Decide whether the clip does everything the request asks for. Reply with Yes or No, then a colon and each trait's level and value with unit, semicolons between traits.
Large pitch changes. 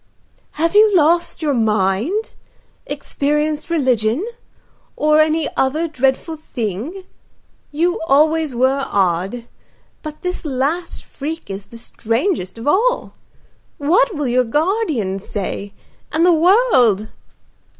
Yes: wide, 6.3 semitones